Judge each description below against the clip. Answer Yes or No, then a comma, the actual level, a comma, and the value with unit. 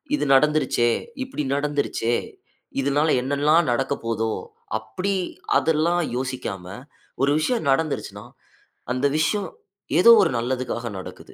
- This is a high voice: No, medium, 145 Hz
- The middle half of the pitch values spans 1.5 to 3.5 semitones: No, average, 4.3 semitones